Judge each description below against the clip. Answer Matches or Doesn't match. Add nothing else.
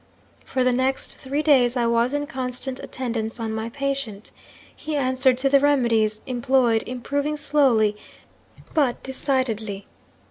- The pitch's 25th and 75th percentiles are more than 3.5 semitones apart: Doesn't match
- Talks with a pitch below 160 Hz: Doesn't match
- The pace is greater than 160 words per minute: Doesn't match